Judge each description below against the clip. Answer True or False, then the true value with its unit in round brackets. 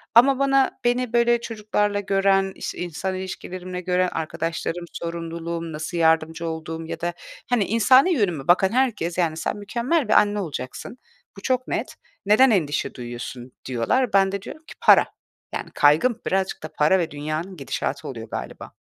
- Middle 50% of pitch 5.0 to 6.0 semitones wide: True (5.3 semitones)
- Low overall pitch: False (185 Hz)